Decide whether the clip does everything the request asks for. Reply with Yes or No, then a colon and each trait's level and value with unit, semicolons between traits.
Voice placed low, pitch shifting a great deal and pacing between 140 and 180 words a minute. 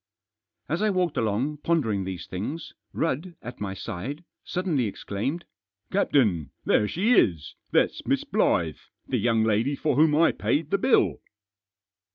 Yes: low, 130 Hz; wide, 8.3 semitones; average, 155 wpm